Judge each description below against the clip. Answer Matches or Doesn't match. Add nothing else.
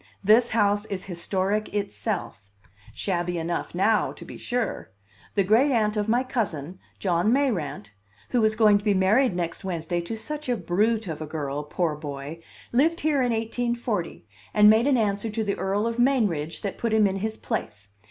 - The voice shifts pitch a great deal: Doesn't match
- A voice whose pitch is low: Doesn't match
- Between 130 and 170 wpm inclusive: Doesn't match